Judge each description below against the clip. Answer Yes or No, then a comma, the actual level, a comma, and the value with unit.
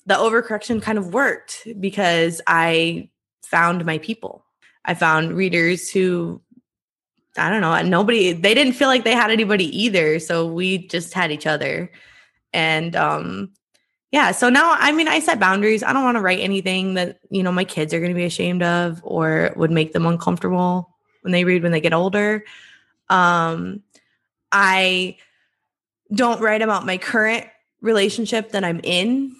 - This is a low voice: No, medium, 185 Hz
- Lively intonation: No, average, 4.2 semitones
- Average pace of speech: Yes, average, 165 wpm